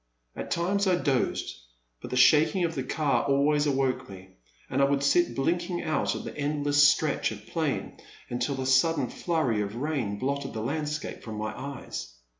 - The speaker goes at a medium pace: Yes, average, 180 wpm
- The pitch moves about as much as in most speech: Yes, average, 3.4 semitones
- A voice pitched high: No, medium, 140 Hz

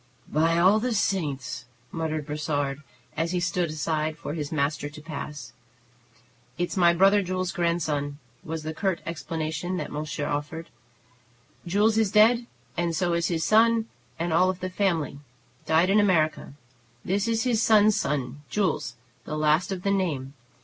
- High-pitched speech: No, medium, 170 Hz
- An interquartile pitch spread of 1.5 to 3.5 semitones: No, average, 3.9 semitones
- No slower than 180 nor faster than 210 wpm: No, average, 155 wpm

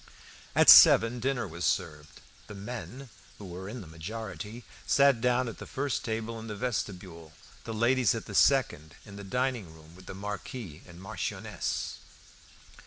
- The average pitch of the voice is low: Yes, low, 110 Hz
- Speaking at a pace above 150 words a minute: Yes, average, 165 wpm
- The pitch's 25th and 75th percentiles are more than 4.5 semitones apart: Yes, average, 5.2 semitones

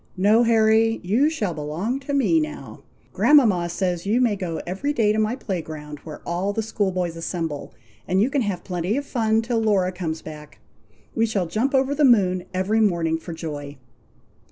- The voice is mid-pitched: No, high, 200 Hz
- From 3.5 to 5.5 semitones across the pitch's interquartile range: Yes, average, 4.9 semitones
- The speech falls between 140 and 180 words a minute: No, average, 190 wpm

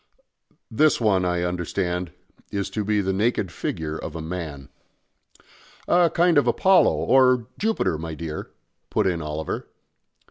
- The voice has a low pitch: Yes, very low, 90 Hz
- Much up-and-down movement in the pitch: Yes, wide, 6.7 semitones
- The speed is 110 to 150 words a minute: Yes, average, 140 wpm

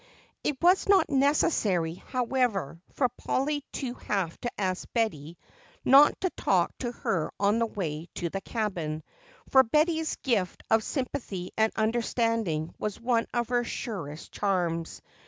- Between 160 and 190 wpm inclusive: No, average, 140 wpm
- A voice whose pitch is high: Yes, high, 225 Hz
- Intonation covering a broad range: Yes, wide, 6.1 semitones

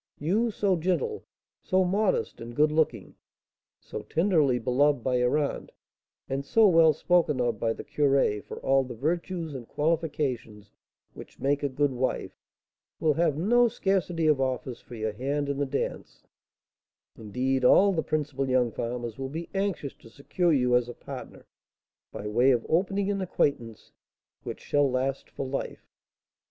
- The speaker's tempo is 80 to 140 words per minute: No, average, 160 wpm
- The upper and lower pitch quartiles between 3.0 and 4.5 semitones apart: No, average, 4.9 semitones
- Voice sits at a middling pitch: Yes, medium, 145 Hz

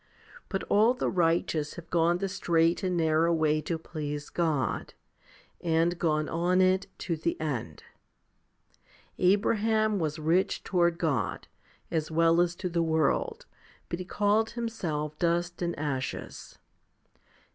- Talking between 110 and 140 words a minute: Yes, slow, 135 wpm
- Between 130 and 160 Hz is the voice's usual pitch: No, medium, 170 Hz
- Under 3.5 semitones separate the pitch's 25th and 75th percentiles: Yes, average, 2.8 semitones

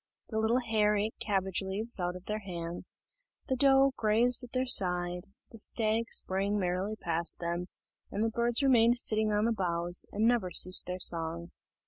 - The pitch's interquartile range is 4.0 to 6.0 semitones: Yes, average, 4.3 semitones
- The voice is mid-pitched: No, high, 210 Hz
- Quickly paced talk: No, average, 175 wpm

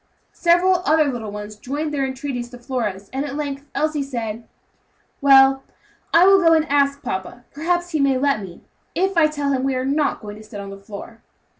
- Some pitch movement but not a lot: Yes, average, 4.5 semitones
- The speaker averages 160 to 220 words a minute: Yes, average, 200 wpm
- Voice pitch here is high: Yes, very high, 275 Hz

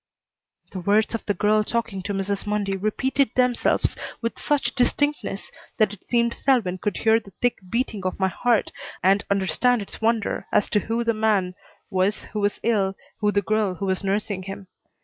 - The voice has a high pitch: Yes, high, 210 Hz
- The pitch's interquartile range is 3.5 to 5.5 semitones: No, average, 3.0 semitones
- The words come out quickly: No, average, 185 wpm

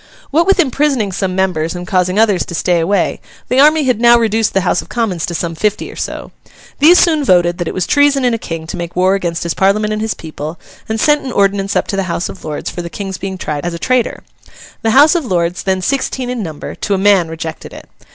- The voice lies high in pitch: Yes, high, 195 Hz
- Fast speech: Yes, fast, 250 wpm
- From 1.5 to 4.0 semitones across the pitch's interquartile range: No, wide, 5.6 semitones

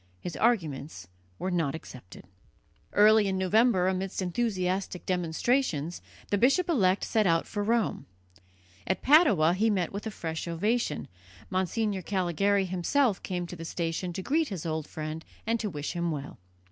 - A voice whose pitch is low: No, medium, 185 Hz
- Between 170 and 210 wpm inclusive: No, average, 155 wpm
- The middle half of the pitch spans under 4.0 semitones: No, average, 4.5 semitones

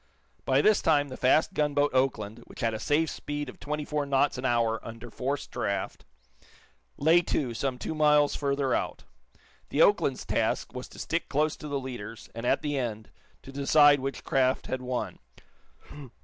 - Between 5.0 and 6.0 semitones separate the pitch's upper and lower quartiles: No, average, 2.9 semitones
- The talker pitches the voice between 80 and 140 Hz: Yes, low, 135 Hz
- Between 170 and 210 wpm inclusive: Yes, average, 175 wpm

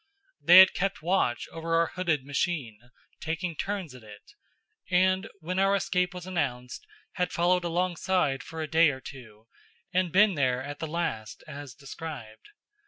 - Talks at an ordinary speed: Yes, average, 165 wpm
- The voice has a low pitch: No, medium, 165 Hz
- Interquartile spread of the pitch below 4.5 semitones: No, average, 5.1 semitones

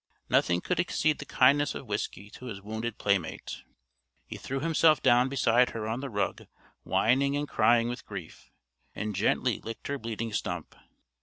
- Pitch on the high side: No, low, 120 Hz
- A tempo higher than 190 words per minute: No, average, 165 wpm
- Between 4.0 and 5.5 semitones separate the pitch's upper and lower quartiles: Yes, average, 4.3 semitones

